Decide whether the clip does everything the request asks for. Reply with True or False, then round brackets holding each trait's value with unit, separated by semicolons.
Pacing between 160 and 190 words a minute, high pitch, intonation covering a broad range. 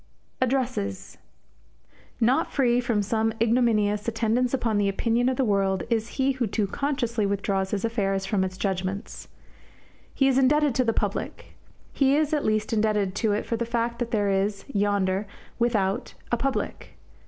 False (165 wpm; 225 Hz; 3.5 semitones)